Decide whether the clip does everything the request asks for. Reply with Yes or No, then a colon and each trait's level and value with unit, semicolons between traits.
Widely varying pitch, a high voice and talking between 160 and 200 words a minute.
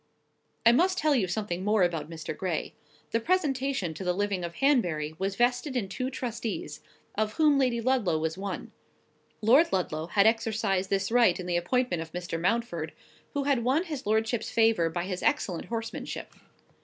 Yes: wide, 5.9 semitones; high, 215 Hz; average, 175 wpm